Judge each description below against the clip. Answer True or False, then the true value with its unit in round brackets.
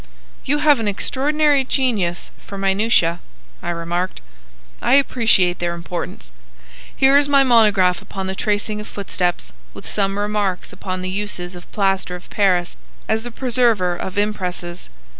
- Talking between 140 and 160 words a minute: True (145 wpm)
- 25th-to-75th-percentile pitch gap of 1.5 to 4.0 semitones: False (4.4 semitones)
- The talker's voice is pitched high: True (200 Hz)